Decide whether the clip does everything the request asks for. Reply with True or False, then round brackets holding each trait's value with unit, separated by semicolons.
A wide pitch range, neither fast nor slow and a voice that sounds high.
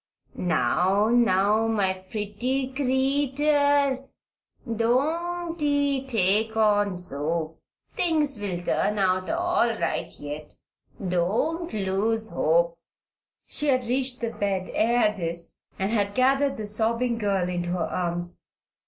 False (6.1 semitones; 115 wpm; 220 Hz)